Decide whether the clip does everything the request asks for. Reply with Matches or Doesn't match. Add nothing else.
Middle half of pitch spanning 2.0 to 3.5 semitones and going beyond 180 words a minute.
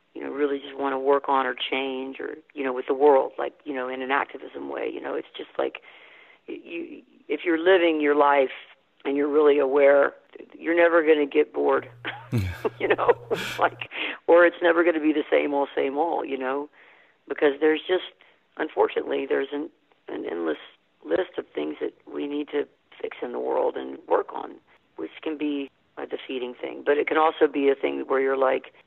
Doesn't match